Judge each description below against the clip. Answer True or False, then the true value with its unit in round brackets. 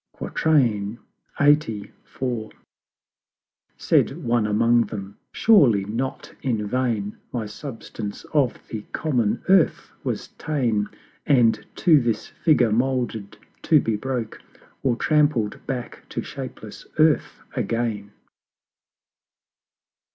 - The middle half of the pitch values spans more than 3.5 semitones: True (4.2 semitones)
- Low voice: True (120 Hz)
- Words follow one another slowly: True (95 wpm)